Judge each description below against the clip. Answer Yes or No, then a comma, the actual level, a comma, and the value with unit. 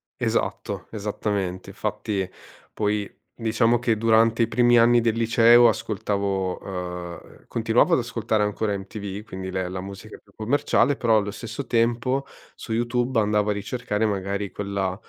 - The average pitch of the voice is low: Yes, low, 105 Hz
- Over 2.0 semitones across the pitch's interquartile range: Yes, average, 2.7 semitones